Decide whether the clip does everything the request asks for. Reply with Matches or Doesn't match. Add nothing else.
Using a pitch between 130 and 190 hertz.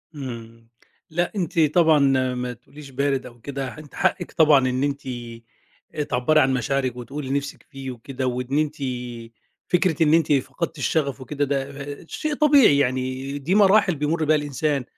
Matches